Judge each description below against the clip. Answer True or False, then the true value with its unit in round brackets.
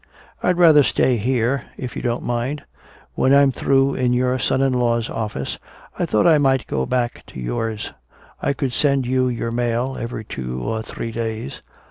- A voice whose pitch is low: True (125 Hz)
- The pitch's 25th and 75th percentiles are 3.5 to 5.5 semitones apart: False (2.7 semitones)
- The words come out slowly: False (180 wpm)